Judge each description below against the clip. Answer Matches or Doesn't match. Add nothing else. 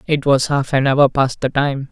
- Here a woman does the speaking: Doesn't match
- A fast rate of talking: Matches